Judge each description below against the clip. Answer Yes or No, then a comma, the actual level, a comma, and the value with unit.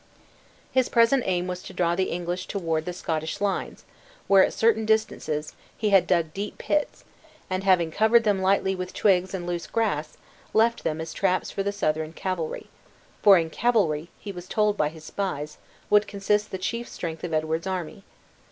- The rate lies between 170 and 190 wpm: Yes, average, 180 wpm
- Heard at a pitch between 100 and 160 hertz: No, medium, 185 Hz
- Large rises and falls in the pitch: No, average, 3.9 semitones